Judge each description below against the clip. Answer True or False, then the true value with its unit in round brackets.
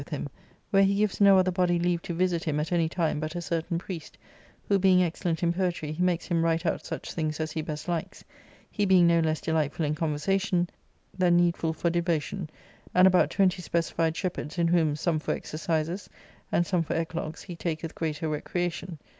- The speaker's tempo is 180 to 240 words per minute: True (190 wpm)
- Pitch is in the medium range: True (170 Hz)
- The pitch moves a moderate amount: False (2.1 semitones)